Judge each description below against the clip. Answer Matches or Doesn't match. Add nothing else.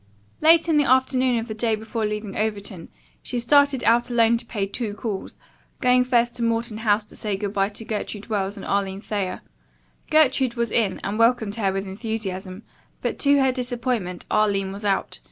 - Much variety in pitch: Doesn't match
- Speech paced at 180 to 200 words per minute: Matches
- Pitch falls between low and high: Doesn't match